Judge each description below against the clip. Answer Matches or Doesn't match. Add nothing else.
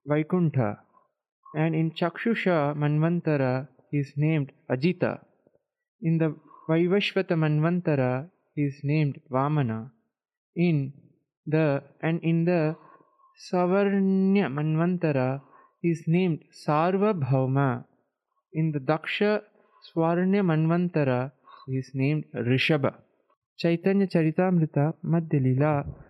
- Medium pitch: Matches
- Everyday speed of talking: Doesn't match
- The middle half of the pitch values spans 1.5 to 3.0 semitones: Doesn't match